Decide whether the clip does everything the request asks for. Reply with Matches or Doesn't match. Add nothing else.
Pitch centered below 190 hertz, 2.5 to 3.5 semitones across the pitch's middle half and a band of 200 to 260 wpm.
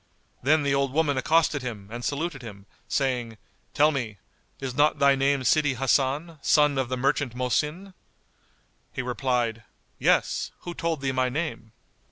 Doesn't match